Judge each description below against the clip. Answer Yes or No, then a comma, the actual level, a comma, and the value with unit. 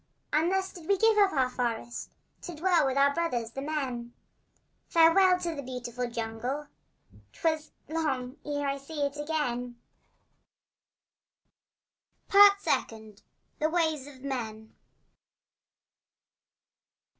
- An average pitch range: Yes, average, 4.7 semitones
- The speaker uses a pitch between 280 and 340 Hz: Yes, very high, 285 Hz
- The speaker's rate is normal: No, slow, 115 wpm